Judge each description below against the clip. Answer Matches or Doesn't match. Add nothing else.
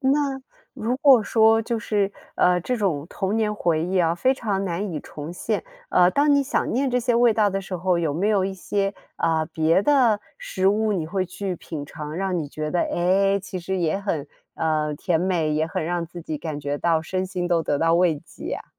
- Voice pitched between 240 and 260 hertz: Doesn't match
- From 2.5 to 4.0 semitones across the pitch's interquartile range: Doesn't match